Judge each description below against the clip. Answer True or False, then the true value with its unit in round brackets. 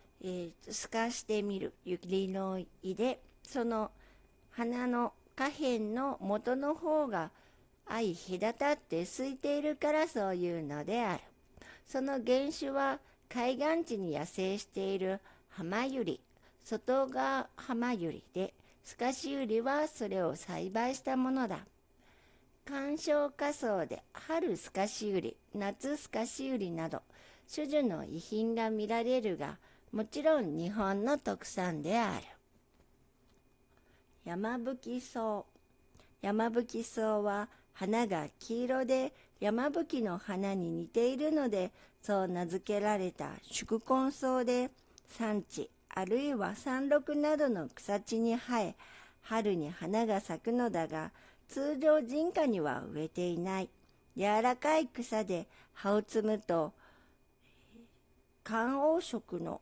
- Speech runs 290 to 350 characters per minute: False (215 characters per minute)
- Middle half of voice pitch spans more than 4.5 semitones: True (5.4 semitones)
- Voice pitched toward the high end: True (230 Hz)